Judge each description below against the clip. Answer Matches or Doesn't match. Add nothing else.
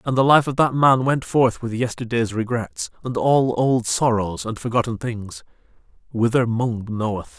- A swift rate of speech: Doesn't match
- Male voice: Matches